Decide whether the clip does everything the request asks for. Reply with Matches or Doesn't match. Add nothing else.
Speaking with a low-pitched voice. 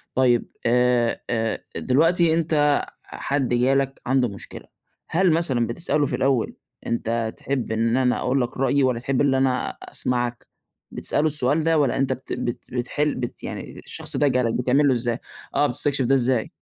Matches